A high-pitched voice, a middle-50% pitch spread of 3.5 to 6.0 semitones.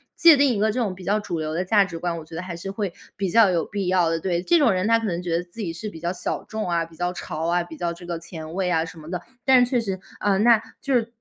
No: medium, 180 Hz; average, 4.0 semitones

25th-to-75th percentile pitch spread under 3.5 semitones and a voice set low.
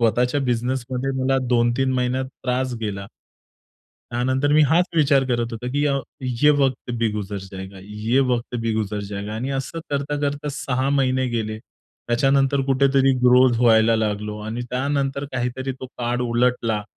Yes: average, 2.7 semitones; low, 125 Hz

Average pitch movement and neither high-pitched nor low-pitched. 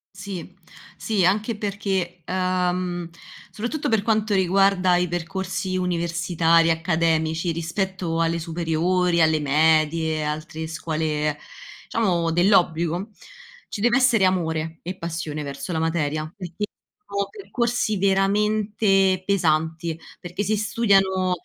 Yes: average, 3.2 semitones; medium, 180 Hz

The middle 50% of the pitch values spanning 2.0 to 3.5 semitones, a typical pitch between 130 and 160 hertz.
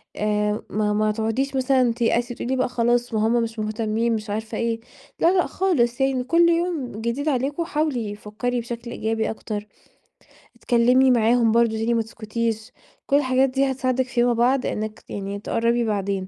No: average, 2.9 semitones; high, 235 Hz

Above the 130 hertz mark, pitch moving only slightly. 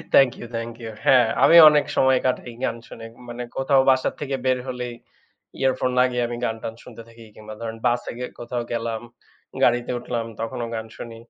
No: low, 120 Hz; narrow, 1.8 semitones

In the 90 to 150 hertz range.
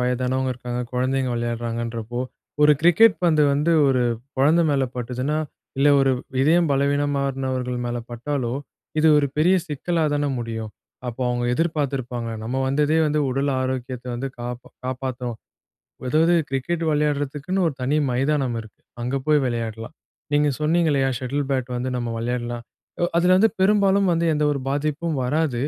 Yes: low, 135 Hz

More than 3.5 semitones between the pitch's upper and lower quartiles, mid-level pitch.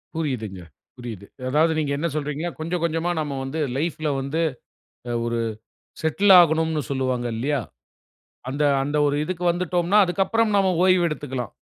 Yes: average, 4.1 semitones; medium, 155 Hz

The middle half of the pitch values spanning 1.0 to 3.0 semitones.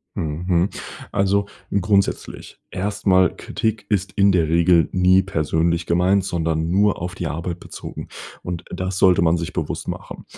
Yes: narrow, 2.5 semitones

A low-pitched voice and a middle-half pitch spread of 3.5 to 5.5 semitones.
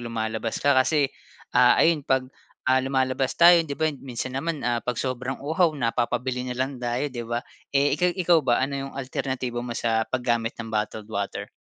No: low, 130 Hz; average, 2.7 semitones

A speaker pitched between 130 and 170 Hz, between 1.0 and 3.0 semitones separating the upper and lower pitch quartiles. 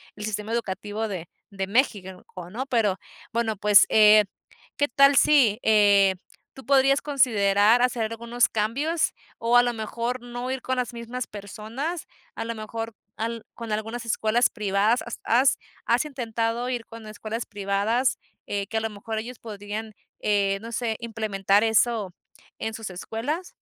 No: high, 225 Hz; narrow, 2.6 semitones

